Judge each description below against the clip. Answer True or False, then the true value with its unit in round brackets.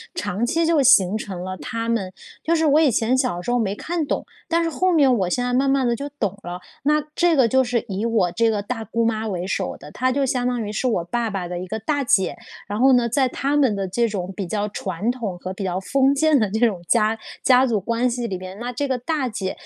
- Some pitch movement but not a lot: True (4.9 semitones)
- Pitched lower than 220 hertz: False (230 Hz)